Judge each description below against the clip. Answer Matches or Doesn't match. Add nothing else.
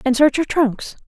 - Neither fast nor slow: Doesn't match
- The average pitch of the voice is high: Matches